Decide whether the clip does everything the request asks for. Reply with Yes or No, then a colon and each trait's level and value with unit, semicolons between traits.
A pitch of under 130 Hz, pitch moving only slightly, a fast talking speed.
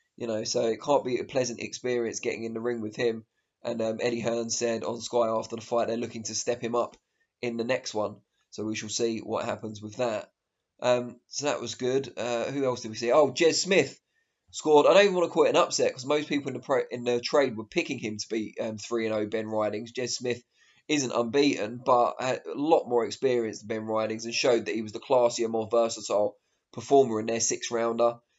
Yes: low, 120 Hz; narrow, 2.1 semitones; fast, 235 wpm